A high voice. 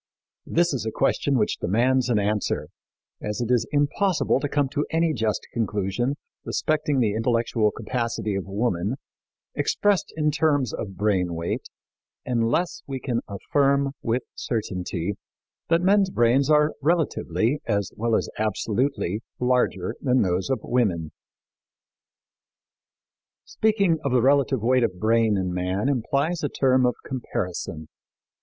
No: low, 120 Hz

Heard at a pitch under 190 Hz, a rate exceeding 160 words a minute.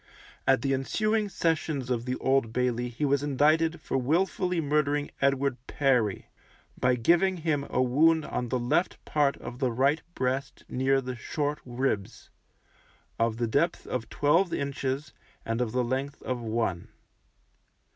No: low, 135 Hz; average, 150 wpm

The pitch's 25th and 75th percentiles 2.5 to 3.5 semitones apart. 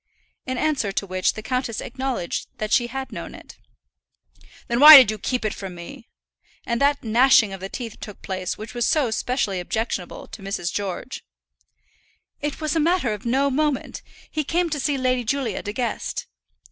No: average, 5.0 semitones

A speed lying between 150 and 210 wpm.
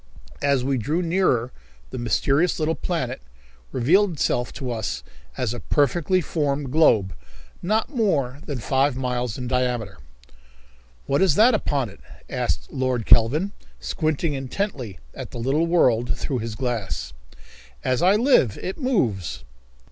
No: average, 140 wpm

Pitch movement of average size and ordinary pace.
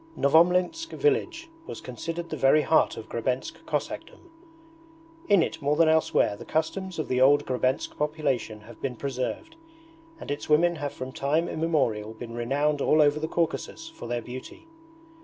Yes: average, 4.5 semitones; average, 160 wpm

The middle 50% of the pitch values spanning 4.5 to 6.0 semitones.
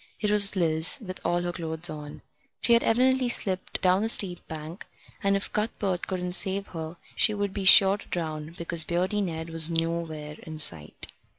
No: average, 3.6 semitones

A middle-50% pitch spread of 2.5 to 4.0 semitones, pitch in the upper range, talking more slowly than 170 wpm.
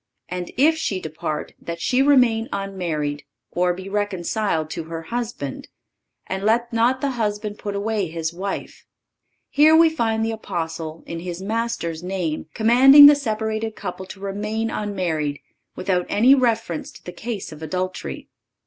No: average, 4.9 semitones; high, 200 Hz; average, 150 wpm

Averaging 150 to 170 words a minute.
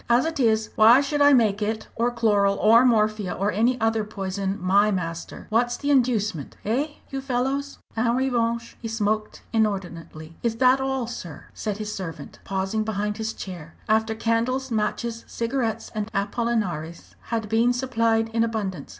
Yes: average, 160 wpm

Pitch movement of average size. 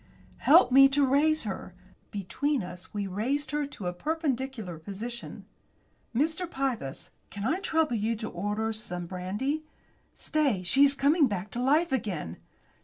No: wide, 6.3 semitones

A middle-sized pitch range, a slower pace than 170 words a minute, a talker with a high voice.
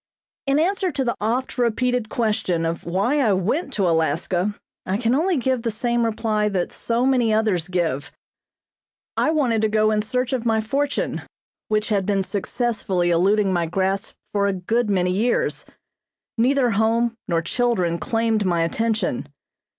Yes: average, 4.3 semitones; average, 160 wpm; high, 215 Hz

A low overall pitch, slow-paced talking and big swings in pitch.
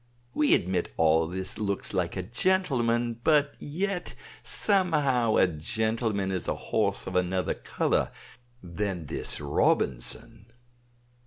Yes: low, 105 Hz; slow, 115 wpm; wide, 6.5 semitones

